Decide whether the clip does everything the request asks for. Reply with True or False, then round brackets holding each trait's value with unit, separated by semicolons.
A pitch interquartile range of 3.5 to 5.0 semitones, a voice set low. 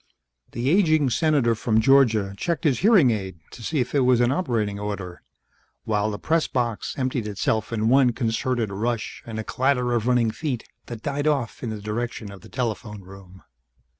True (4.0 semitones; 120 Hz)